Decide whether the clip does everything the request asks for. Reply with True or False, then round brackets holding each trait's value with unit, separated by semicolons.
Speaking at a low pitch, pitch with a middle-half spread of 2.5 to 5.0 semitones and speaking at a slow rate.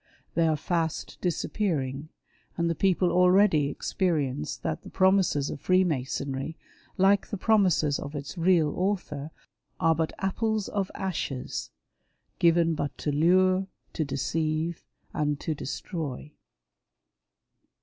False (165 Hz; 4.1 semitones; 120 wpm)